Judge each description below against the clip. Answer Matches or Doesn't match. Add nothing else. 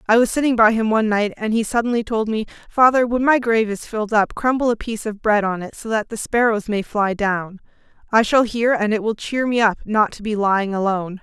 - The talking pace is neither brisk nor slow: Doesn't match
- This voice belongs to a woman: Matches